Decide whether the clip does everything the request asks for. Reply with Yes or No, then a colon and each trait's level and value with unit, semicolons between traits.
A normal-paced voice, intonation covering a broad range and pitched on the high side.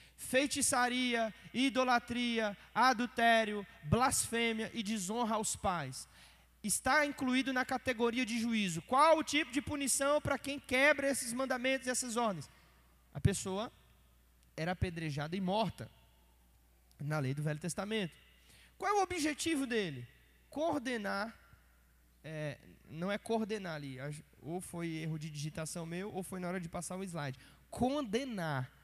Yes: average, 135 wpm; wide, 8.5 semitones; high, 215 Hz